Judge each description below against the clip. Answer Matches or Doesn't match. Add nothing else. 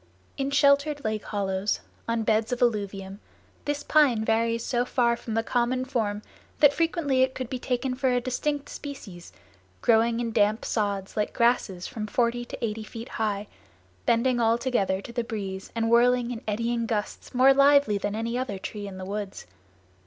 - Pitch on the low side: Doesn't match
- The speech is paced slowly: Doesn't match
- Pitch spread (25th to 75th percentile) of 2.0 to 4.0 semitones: Matches